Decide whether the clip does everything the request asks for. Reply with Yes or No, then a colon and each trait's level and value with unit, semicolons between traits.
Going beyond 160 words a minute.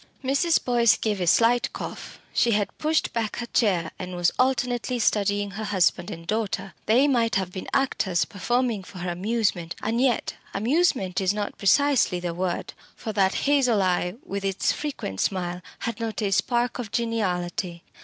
Yes: average, 170 wpm